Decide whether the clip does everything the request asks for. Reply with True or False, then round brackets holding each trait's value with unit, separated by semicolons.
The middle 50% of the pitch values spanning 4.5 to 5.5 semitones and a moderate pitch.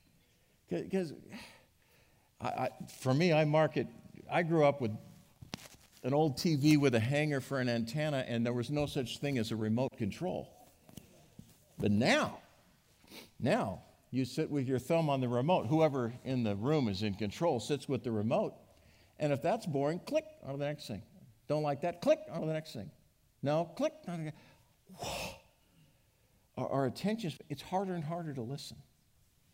True (4.8 semitones; 145 Hz)